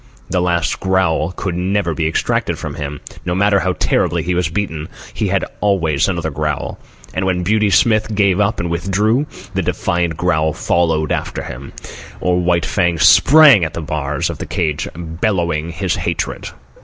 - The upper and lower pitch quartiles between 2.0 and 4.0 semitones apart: Yes, average, 3.1 semitones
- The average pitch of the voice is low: Yes, very low, 90 Hz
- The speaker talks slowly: No, average, 170 wpm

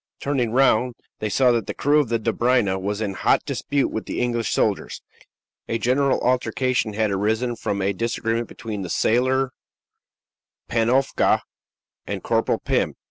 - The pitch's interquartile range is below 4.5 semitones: Yes, average, 2.9 semitones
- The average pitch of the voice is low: Yes, low, 120 Hz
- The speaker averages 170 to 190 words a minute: No, average, 150 wpm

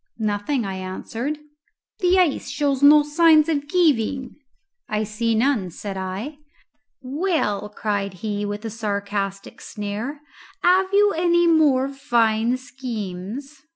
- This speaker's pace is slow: Yes, slow, 120 wpm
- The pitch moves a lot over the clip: Yes, wide, 6.3 semitones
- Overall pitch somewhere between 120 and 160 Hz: No, high, 240 Hz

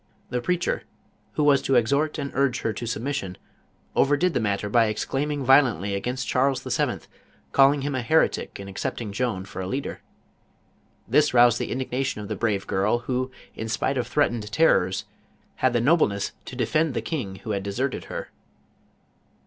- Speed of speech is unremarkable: Yes, average, 175 wpm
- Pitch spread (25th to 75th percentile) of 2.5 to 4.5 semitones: No, average, 4.9 semitones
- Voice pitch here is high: No, low, 125 Hz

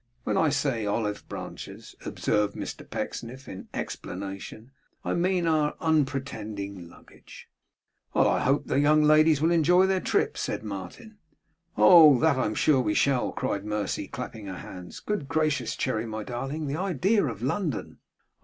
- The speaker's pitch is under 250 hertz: Yes, low, 135 Hz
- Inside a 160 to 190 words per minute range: No, average, 150 wpm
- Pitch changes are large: Yes, wide, 6.8 semitones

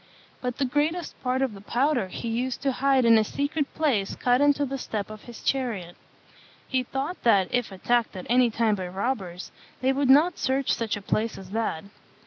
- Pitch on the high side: Yes, high, 245 Hz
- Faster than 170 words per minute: Yes, average, 200 wpm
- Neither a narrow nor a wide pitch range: Yes, average, 4.2 semitones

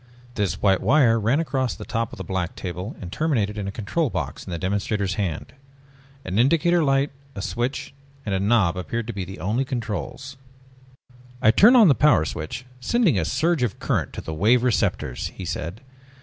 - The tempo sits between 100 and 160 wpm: No, average, 190 wpm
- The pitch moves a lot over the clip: Yes, wide, 6.0 semitones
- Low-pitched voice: Yes, low, 110 Hz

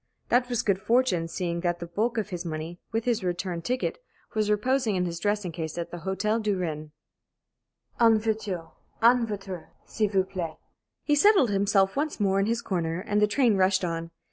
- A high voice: Yes, high, 195 Hz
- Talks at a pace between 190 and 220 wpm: Yes, average, 195 wpm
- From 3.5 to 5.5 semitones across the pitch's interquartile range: Yes, average, 4.4 semitones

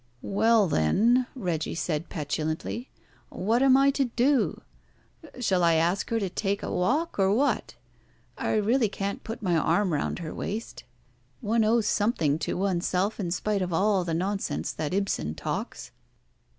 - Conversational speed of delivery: Yes, average, 155 wpm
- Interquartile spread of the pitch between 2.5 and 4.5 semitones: No, average, 5.0 semitones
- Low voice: No, high, 200 Hz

